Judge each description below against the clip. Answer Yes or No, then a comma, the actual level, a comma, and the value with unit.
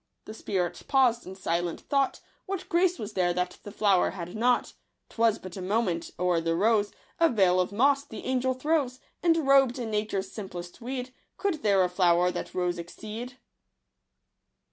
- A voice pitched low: No, high, 215 Hz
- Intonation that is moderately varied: No, wide, 6.1 semitones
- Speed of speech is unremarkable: Yes, average, 175 wpm